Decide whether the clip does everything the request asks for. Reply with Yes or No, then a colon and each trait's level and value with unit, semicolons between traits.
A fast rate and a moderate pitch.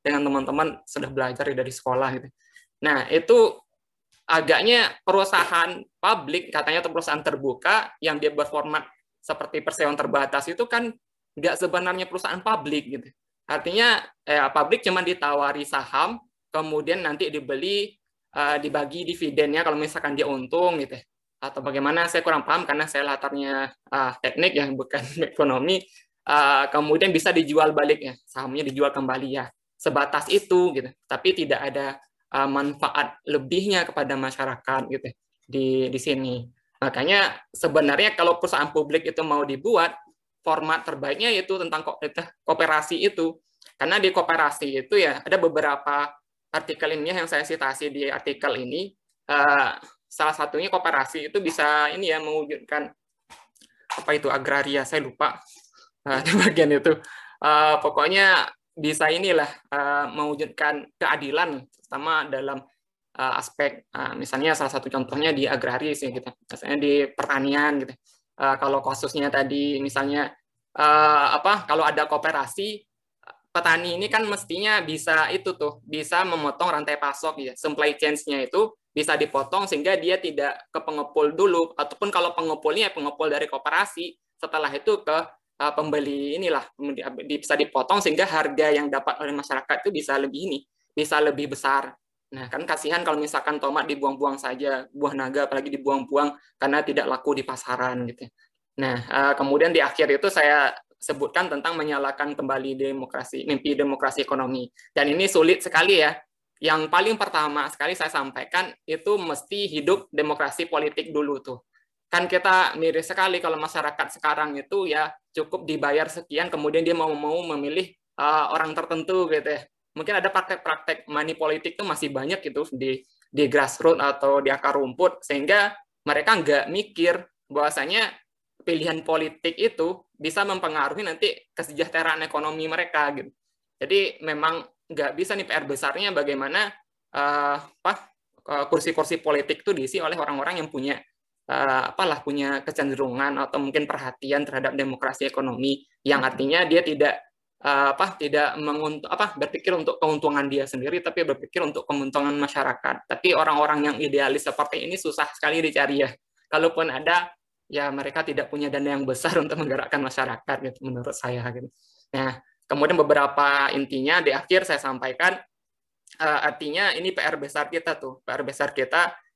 Yes: fast, 150 wpm; medium, 150 Hz